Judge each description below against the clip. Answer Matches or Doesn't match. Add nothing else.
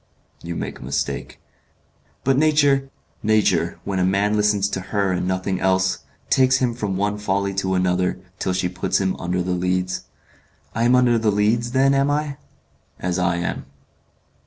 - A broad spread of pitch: Doesn't match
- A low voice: Matches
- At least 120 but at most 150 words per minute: Doesn't match